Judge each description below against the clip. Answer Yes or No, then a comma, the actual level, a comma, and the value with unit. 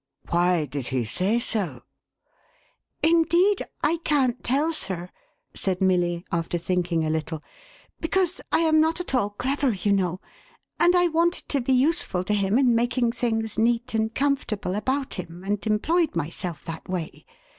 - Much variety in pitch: Yes, wide, 8.2 semitones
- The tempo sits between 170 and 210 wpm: Yes, average, 175 wpm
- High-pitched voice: Yes, high, 220 Hz